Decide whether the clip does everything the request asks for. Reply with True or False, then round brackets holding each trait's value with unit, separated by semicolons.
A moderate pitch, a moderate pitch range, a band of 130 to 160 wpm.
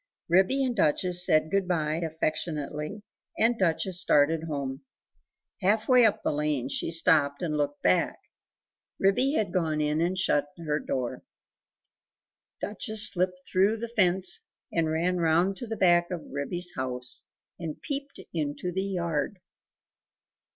True (175 Hz; 4.1 semitones; 140 wpm)